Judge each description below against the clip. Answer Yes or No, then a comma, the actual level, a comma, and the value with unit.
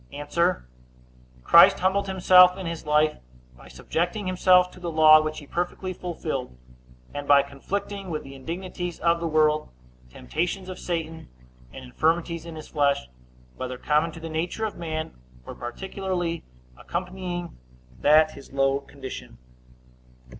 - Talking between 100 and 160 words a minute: Yes, average, 140 wpm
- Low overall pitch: No, medium, 165 Hz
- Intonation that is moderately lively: Yes, average, 3.6 semitones